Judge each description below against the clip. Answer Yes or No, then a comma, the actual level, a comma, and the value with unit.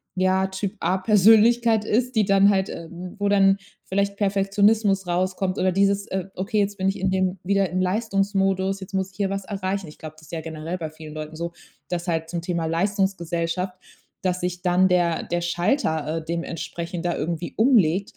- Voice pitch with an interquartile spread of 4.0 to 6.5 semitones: No, narrow, 2.5 semitones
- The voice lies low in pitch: No, medium, 185 Hz